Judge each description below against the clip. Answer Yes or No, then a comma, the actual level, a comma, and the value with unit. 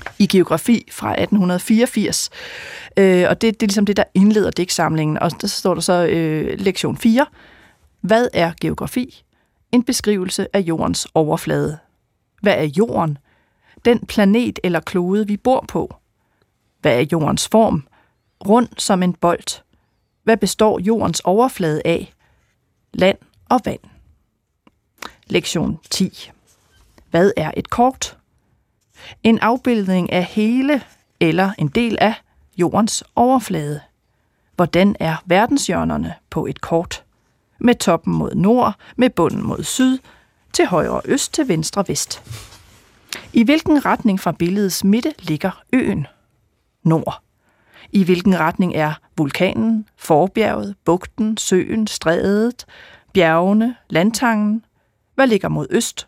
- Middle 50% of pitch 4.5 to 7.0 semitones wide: Yes, average, 5.2 semitones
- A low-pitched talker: No, high, 195 Hz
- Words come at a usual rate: No, slow, 125 wpm